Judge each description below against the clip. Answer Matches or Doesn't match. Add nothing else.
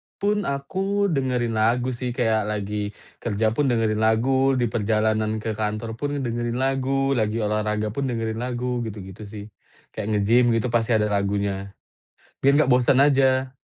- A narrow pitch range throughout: Doesn't match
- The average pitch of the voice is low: Matches